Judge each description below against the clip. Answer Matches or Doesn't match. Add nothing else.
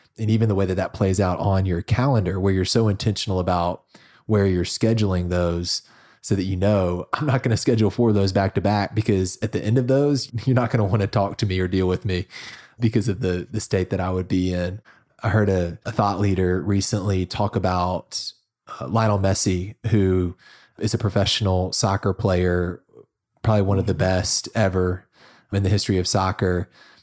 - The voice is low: Matches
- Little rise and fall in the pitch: Doesn't match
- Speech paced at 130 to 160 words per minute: Doesn't match